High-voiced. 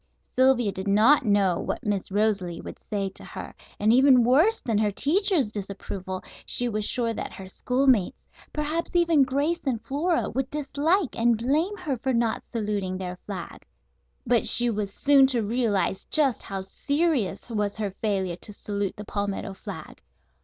Yes: high, 230 Hz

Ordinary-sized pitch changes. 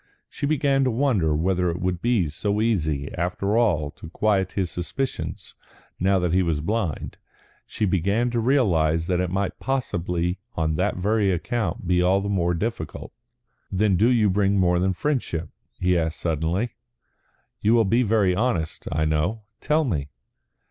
Yes: average, 4.6 semitones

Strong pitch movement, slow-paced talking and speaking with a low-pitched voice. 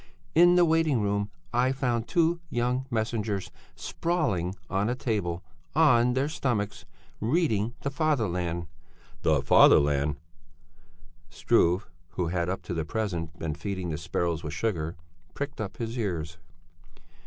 Yes: wide, 7.1 semitones; slow, 130 wpm; low, 105 Hz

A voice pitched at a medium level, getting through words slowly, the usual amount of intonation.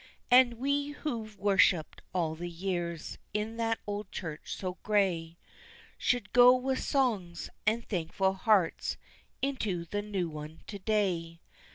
No: high, 200 Hz; slow, 130 wpm; average, 5.0 semitones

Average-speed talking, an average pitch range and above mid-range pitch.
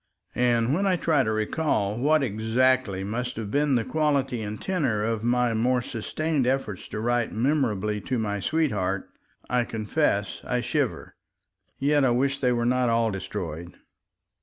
No: average, 160 wpm; average, 4.1 semitones; low, 120 Hz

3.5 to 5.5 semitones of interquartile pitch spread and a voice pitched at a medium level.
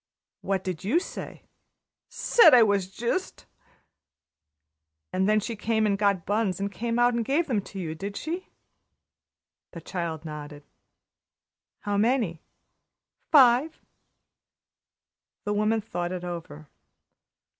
No: average, 4.7 semitones; high, 205 Hz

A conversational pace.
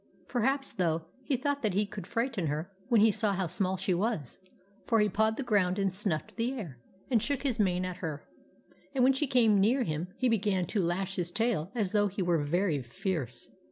No: fast, 215 wpm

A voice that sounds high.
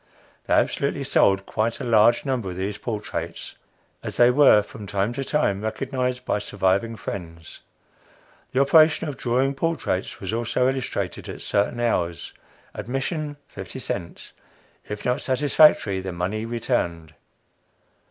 No: low, 115 Hz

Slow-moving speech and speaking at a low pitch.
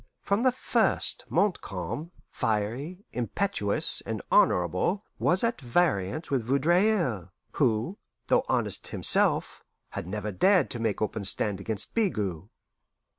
Yes: slow, 120 wpm; low, 120 Hz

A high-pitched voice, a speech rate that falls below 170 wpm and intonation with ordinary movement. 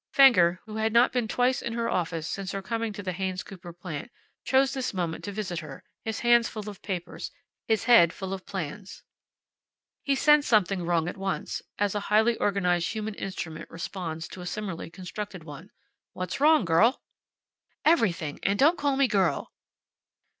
No: high, 200 Hz; average, 175 wpm; average, 4.5 semitones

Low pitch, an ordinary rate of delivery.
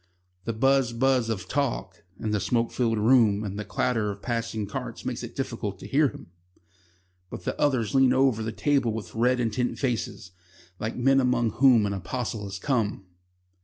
Yes: low, 115 Hz; average, 180 wpm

